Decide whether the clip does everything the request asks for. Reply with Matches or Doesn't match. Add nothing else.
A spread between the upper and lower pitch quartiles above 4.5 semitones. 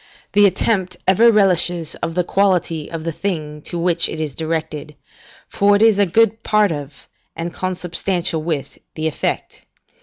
Doesn't match